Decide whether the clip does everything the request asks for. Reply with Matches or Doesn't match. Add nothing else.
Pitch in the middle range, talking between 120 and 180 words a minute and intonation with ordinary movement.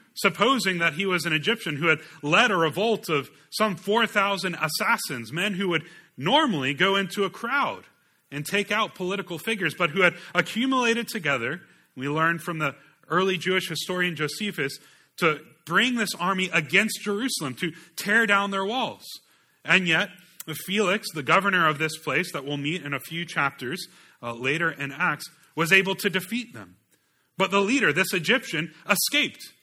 Matches